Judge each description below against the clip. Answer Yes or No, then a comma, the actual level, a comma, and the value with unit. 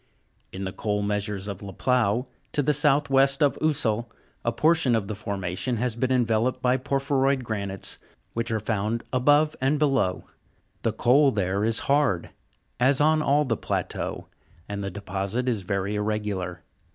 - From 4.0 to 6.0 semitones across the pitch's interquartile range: Yes, average, 5.1 semitones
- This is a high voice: No, low, 115 Hz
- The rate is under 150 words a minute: No, average, 165 wpm